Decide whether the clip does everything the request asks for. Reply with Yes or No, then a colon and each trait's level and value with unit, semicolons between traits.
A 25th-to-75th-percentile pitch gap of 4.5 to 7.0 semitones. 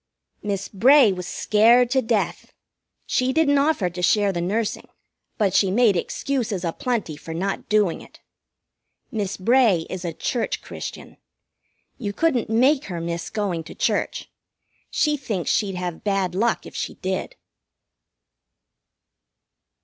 Yes: average, 5.1 semitones